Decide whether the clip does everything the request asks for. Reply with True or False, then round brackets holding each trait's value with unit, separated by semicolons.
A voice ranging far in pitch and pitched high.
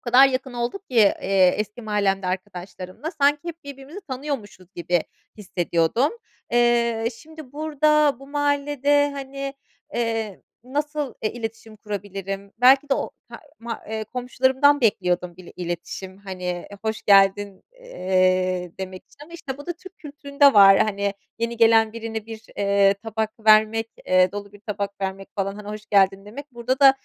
True (5.7 semitones; 220 Hz)